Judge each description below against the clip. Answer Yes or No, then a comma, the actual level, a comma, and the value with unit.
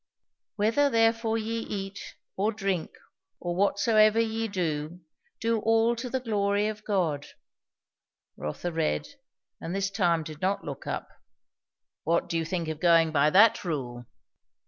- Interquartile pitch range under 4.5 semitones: No, average, 5.3 semitones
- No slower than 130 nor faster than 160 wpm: Yes, average, 145 wpm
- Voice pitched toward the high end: Yes, high, 195 Hz